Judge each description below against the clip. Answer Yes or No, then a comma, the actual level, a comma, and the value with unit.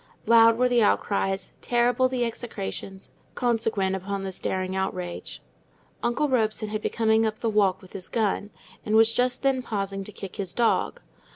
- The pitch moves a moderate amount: Yes, average, 3.5 semitones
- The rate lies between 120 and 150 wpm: No, average, 170 wpm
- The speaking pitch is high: Yes, high, 215 Hz